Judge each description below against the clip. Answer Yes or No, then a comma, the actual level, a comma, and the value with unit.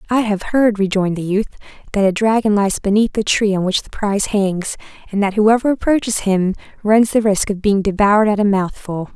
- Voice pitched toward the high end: Yes, high, 205 Hz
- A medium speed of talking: No, fast, 210 wpm